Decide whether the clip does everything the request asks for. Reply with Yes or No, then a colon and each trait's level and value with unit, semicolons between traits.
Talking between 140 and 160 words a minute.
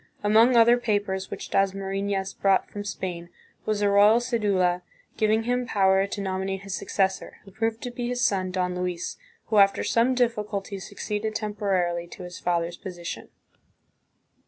Yes: average, 155 wpm